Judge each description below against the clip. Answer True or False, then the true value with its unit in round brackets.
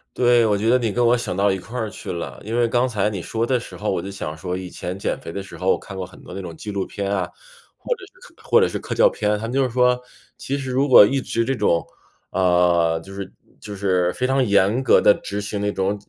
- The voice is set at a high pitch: False (105 Hz)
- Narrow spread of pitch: False (4.5 semitones)